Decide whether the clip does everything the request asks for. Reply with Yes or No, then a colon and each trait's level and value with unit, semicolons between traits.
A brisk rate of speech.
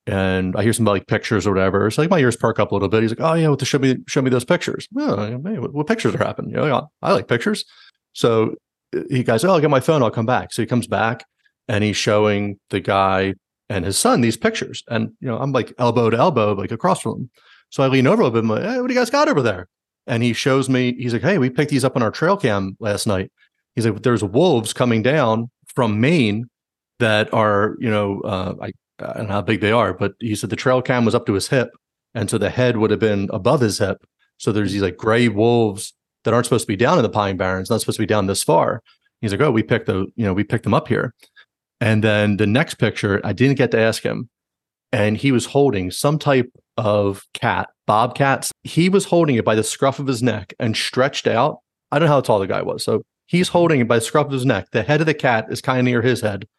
Yes: fast, 265 wpm